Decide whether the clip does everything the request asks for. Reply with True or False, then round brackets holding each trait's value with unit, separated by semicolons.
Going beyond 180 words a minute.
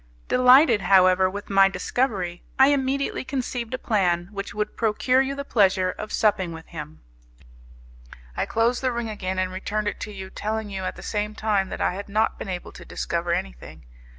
True (190 wpm)